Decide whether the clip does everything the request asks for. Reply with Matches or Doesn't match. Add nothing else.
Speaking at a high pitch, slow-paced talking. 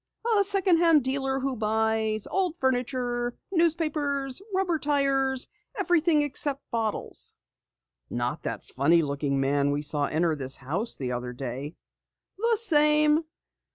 Matches